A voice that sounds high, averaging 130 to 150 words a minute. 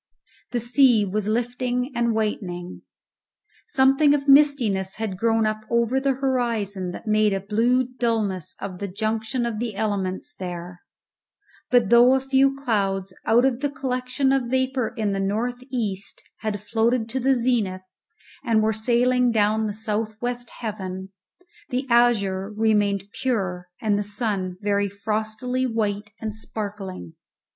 Yes: high, 220 Hz; average, 145 wpm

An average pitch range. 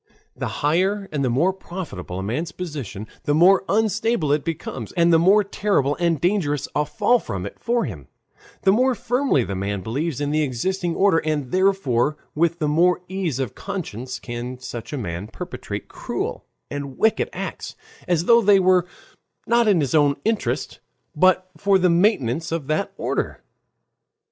No: wide, 6.4 semitones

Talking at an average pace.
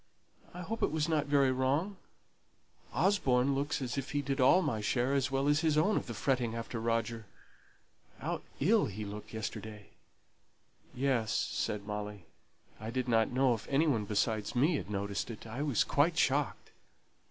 Yes: average, 165 wpm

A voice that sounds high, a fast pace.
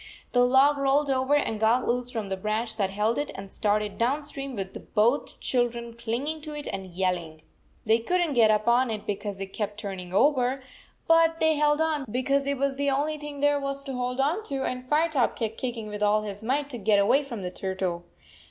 Yes: high, 245 Hz; fast, 225 wpm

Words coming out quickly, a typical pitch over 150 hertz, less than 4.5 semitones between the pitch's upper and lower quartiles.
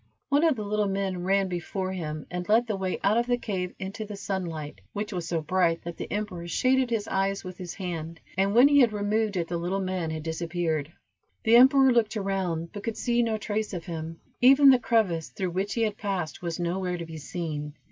Yes: fast, 225 wpm; high, 190 Hz; average, 4.1 semitones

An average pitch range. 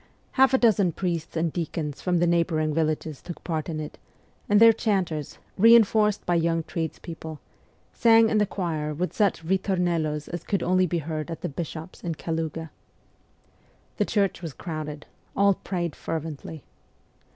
Yes: average, 3.3 semitones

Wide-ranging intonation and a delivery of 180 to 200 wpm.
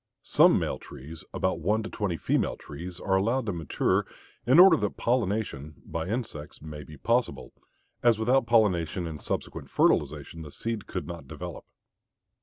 No: wide, 6.4 semitones; average, 160 wpm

